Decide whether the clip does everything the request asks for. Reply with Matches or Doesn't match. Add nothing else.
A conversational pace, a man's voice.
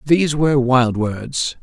Matches